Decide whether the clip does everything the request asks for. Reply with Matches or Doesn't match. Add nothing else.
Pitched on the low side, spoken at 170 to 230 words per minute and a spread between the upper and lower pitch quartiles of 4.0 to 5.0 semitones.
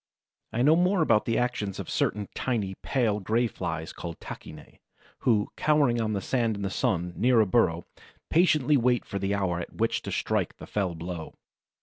Matches